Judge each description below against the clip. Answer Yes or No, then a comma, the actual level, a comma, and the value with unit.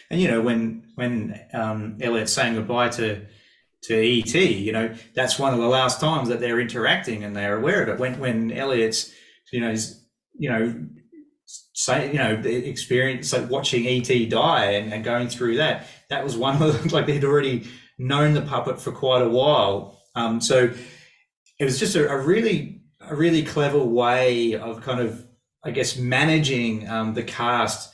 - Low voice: Yes, low, 120 Hz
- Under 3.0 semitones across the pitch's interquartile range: Yes, narrow, 2.5 semitones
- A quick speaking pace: No, average, 185 wpm